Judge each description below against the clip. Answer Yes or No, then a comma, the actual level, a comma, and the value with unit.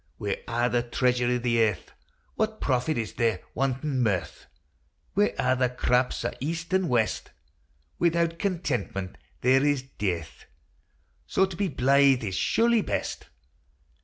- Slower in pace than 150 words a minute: Yes, average, 140 wpm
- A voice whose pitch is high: No, low, 130 Hz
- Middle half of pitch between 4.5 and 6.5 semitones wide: Yes, wide, 5.6 semitones